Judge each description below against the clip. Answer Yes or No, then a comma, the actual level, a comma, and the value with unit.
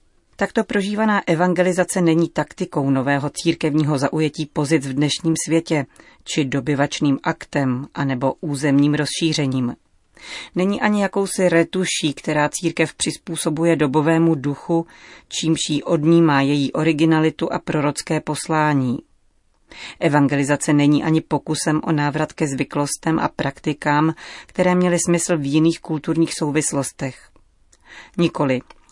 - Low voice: No, medium, 155 Hz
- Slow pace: Yes, slow, 110 wpm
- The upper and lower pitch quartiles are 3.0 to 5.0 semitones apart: No, narrow, 2.5 semitones